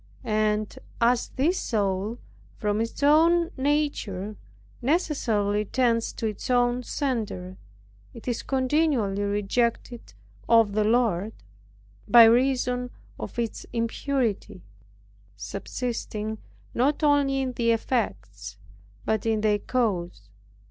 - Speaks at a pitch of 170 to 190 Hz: No, high, 230 Hz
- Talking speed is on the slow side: Yes, slow, 105 wpm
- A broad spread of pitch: No, average, 3.7 semitones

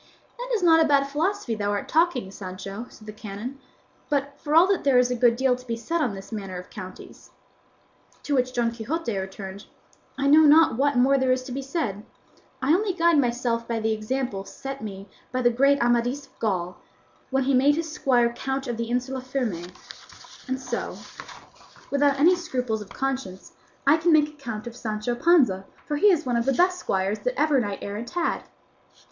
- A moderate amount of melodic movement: Yes, average, 4.7 semitones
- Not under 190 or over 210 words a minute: Yes, average, 200 wpm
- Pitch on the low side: No, very high, 255 Hz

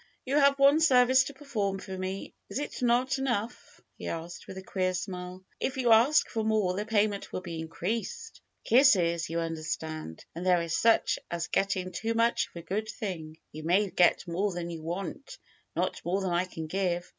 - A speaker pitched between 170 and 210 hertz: Yes, high, 190 Hz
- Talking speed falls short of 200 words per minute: No, fast, 205 wpm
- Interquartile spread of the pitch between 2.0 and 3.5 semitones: No, average, 5.2 semitones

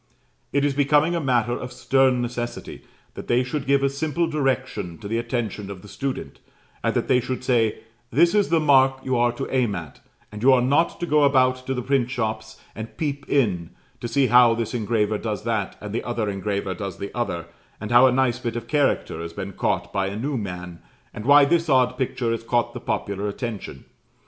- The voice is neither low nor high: No, low, 120 Hz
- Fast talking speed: Yes, fast, 215 wpm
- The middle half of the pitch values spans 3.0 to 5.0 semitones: Yes, average, 4.0 semitones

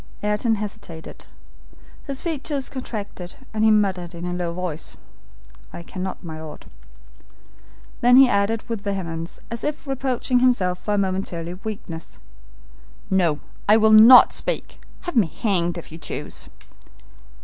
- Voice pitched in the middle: No, high, 200 Hz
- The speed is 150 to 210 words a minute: No, average, 140 wpm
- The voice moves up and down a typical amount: Yes, average, 4.8 semitones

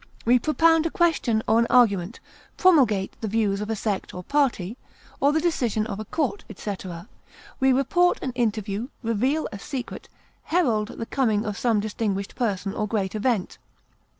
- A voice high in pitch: Yes, high, 225 Hz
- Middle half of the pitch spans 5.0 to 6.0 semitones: No, average, 4.6 semitones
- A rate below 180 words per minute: Yes, average, 165 wpm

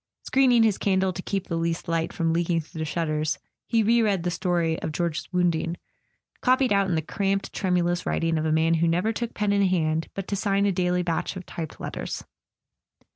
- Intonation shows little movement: No, average, 3.2 semitones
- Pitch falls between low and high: Yes, medium, 180 Hz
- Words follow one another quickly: Yes, fast, 215 wpm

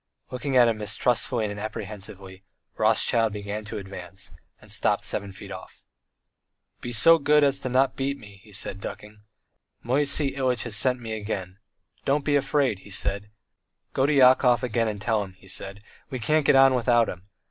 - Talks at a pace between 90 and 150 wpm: No, average, 180 wpm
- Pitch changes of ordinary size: Yes, average, 4.5 semitones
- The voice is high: No, low, 115 Hz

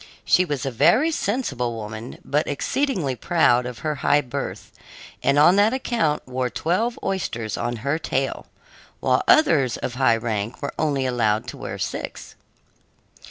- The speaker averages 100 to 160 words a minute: Yes, average, 155 wpm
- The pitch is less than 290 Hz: Yes, medium, 140 Hz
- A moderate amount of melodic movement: No, wide, 6.3 semitones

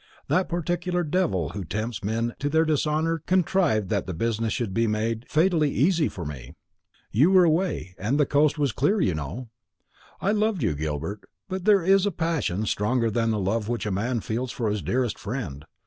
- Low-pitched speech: Yes, low, 120 Hz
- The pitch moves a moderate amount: No, wide, 7.9 semitones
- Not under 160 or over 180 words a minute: No, average, 195 wpm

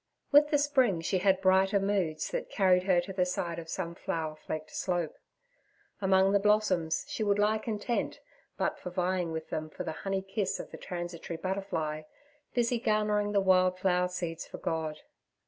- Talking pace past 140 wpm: Yes, average, 180 wpm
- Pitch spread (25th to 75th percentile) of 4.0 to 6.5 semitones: No, average, 3.1 semitones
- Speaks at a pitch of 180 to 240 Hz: Yes, medium, 185 Hz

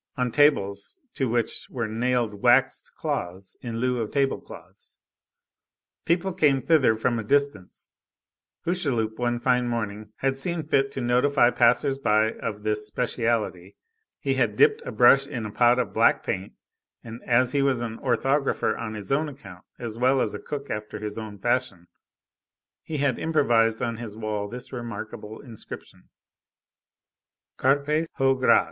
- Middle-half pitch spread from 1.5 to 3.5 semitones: No, average, 3.9 semitones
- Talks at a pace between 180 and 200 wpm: No, average, 155 wpm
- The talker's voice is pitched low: Yes, low, 120 Hz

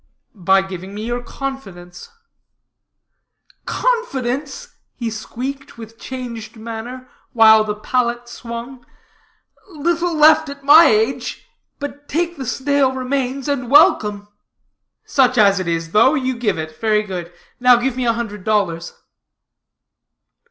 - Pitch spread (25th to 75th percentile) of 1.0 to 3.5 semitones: No, average, 4.4 semitones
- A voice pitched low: No, high, 245 Hz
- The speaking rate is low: Yes, slow, 125 wpm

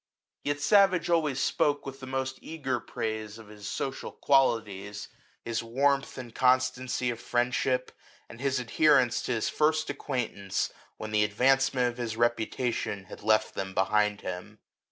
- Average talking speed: Yes, average, 150 wpm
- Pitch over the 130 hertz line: No, low, 125 Hz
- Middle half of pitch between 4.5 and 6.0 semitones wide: No, average, 3.8 semitones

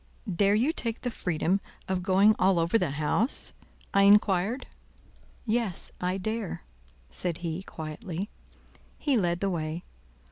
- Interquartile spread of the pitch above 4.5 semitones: No, average, 3.9 semitones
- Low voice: No, high, 190 Hz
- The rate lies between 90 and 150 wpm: Yes, slow, 135 wpm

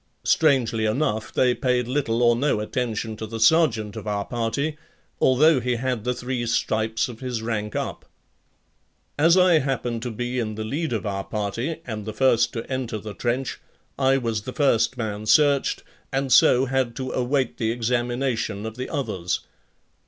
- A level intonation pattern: No, average, 3.1 semitones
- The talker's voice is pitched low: Yes, low, 120 Hz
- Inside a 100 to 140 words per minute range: No, average, 175 wpm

